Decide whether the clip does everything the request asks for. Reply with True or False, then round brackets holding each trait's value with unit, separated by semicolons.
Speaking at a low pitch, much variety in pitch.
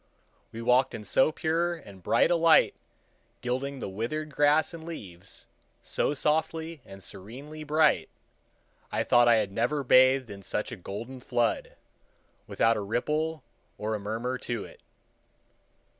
True (130 Hz; 5.7 semitones)